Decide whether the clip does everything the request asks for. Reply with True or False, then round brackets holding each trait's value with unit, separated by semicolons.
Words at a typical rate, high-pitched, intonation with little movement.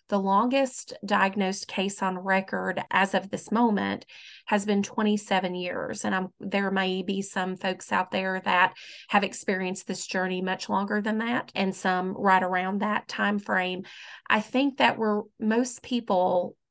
True (160 wpm; 195 Hz; 2.0 semitones)